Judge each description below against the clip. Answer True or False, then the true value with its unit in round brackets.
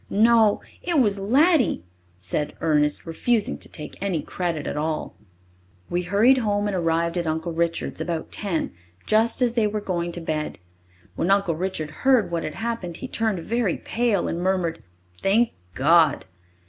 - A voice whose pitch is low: False (185 Hz)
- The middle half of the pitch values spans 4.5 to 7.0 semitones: True (5.1 semitones)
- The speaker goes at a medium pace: True (160 wpm)